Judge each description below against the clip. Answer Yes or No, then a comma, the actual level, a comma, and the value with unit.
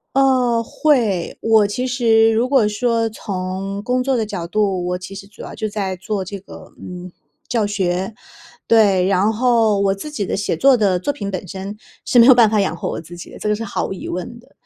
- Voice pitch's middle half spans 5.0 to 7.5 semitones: No, average, 3.5 semitones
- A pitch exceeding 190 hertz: Yes, high, 210 Hz